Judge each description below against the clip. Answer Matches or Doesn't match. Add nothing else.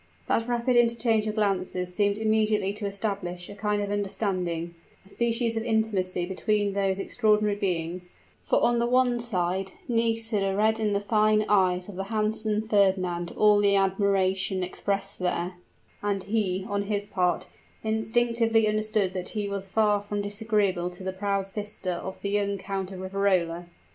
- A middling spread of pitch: Doesn't match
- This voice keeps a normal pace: Matches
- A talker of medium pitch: Doesn't match